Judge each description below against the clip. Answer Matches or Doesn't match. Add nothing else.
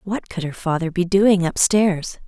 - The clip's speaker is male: Doesn't match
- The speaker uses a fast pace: Matches